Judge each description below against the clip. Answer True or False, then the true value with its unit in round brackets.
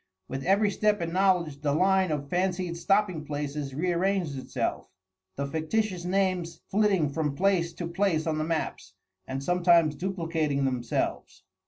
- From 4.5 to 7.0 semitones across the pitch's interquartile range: False (4.1 semitones)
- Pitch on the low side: False (170 Hz)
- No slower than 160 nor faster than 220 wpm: False (145 wpm)